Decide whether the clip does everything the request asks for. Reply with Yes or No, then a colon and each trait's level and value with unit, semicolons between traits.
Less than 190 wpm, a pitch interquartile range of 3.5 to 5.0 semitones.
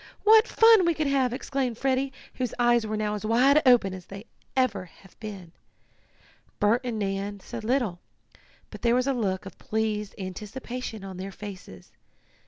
Yes: average, 170 wpm; average, 4.5 semitones